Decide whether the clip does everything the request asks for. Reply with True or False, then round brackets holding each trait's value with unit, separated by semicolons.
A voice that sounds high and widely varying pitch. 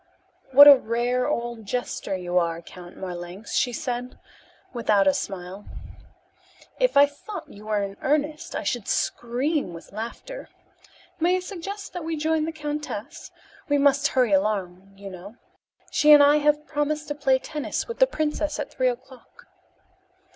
True (255 Hz; 7.0 semitones)